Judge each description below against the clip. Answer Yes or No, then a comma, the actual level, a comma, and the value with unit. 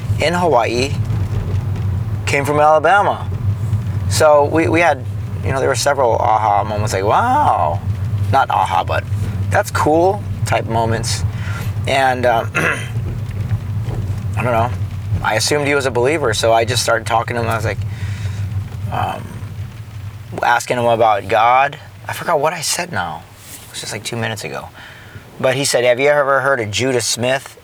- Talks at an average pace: Yes, average, 160 wpm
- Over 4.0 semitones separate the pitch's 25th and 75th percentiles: No, narrow, 2.5 semitones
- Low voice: Yes, low, 110 Hz